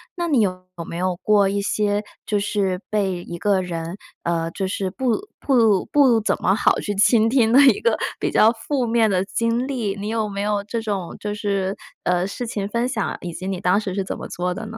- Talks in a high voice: Yes, high, 205 Hz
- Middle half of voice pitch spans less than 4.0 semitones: Yes, average, 3.3 semitones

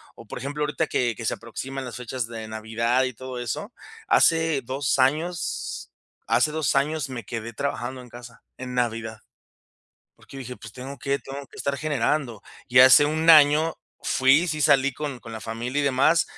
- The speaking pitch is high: No, low, 130 Hz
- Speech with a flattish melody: No, average, 3.4 semitones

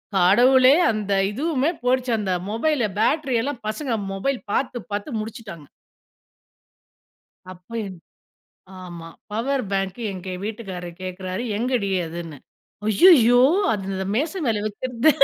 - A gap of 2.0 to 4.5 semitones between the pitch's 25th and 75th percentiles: No, average, 5.2 semitones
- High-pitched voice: Yes, high, 220 Hz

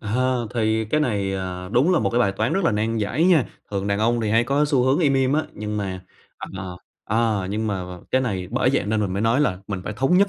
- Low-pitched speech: Yes, low, 110 Hz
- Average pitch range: Yes, average, 4.6 semitones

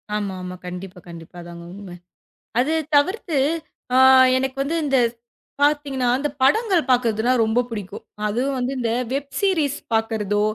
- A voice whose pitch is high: Yes, very high, 250 Hz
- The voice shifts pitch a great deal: Yes, wide, 5.9 semitones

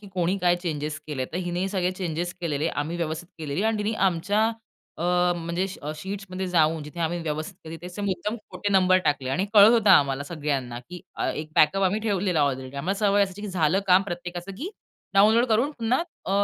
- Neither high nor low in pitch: Yes, medium, 180 Hz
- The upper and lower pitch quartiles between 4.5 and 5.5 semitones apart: No, average, 4.1 semitones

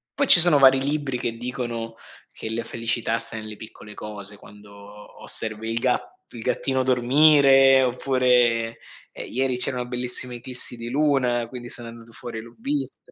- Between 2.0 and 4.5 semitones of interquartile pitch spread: Yes, narrow, 2.5 semitones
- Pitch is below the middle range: Yes, low, 125 Hz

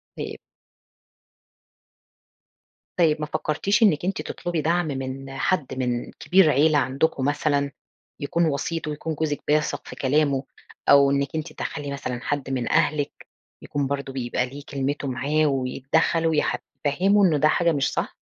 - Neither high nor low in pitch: Yes, medium, 145 Hz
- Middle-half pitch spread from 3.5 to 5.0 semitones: No, average, 2.7 semitones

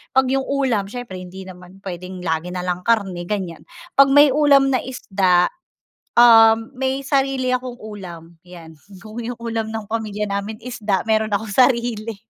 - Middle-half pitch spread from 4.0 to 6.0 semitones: Yes, average, 4.9 semitones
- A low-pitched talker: No, high, 220 Hz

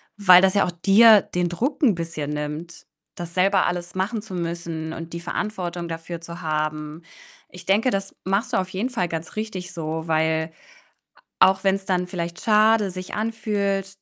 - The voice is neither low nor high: Yes, medium, 180 Hz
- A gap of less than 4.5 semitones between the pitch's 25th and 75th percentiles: Yes, average, 2.9 semitones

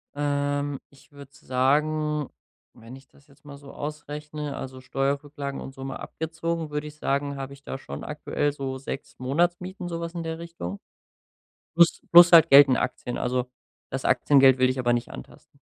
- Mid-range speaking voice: Yes, medium, 145 Hz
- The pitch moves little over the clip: Yes, narrow, 2.2 semitones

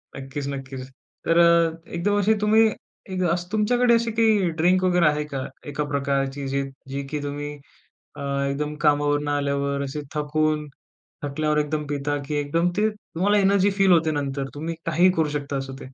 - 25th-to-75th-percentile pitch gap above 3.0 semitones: Yes, average, 4.5 semitones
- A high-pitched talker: No, medium, 150 Hz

